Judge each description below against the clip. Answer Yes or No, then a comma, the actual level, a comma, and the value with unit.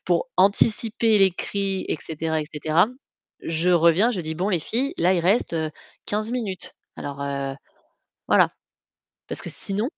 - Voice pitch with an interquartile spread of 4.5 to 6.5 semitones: Yes, average, 4.9 semitones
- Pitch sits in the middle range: Yes, medium, 180 Hz